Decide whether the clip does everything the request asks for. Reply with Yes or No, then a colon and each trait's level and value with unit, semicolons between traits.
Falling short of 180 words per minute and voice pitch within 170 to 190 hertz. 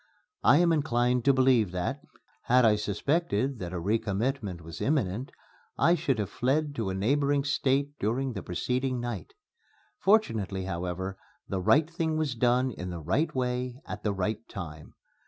No: average, 160 wpm; low, 120 Hz